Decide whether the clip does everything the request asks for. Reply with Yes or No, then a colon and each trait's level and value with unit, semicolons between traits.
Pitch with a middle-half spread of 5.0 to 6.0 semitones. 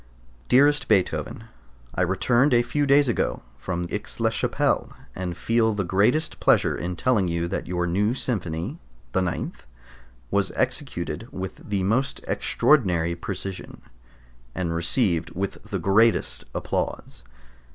Yes: wide, 5.6 semitones